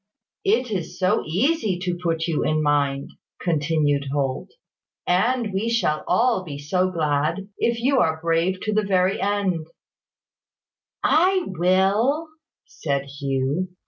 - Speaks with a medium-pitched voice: Yes, medium, 180 Hz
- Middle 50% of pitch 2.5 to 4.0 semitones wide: No, wide, 5.5 semitones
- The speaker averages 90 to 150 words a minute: Yes, slow, 135 wpm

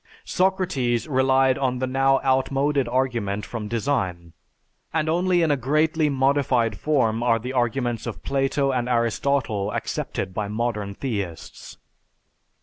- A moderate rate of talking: No, slow, 130 wpm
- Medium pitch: No, low, 130 Hz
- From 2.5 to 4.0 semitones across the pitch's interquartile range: Yes, average, 3.3 semitones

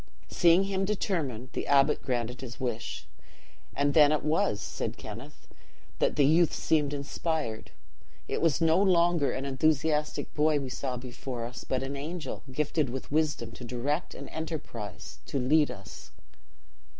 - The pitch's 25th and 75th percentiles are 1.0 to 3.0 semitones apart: No, average, 4.0 semitones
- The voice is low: No, medium, 145 Hz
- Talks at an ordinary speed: Yes, average, 150 wpm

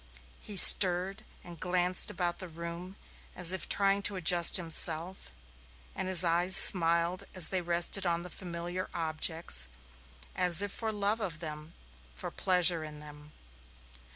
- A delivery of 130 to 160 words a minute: Yes, average, 145 wpm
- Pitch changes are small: Yes, narrow, 1.9 semitones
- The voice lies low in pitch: No, medium, 175 Hz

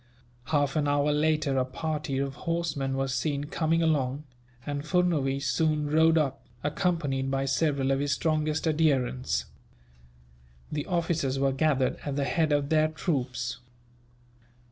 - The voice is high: No, medium, 145 Hz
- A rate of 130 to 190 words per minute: Yes, average, 140 wpm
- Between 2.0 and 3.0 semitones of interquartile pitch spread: Yes, narrow, 2.6 semitones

